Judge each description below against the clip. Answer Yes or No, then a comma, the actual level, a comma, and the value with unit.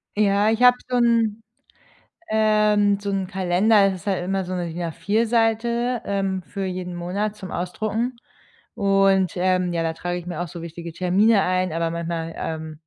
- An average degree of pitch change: Yes, average, 3.3 semitones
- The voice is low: No, high, 190 Hz